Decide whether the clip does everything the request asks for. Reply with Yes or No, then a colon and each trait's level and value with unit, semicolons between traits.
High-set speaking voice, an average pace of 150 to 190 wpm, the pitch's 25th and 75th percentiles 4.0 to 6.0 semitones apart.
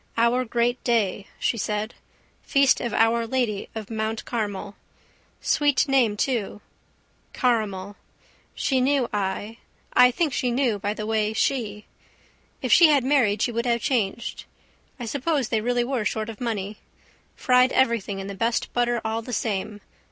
No: high, 230 Hz; average, 155 wpm; average, 3.0 semitones